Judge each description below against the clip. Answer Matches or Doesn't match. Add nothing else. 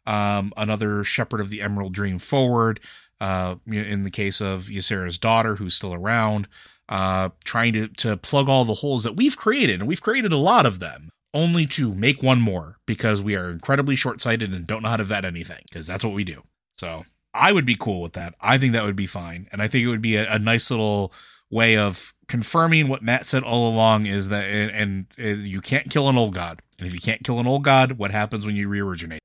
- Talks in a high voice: Doesn't match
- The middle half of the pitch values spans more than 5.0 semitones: Doesn't match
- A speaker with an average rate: Doesn't match